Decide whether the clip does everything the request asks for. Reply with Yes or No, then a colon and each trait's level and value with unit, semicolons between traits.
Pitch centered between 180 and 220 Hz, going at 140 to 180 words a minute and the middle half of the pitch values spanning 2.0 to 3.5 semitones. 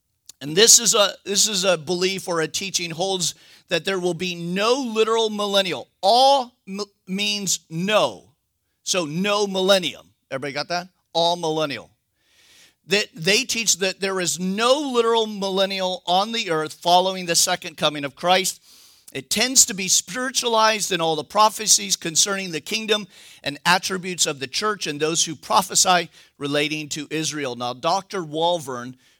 No: medium, 185 Hz; average, 160 wpm; average, 4.1 semitones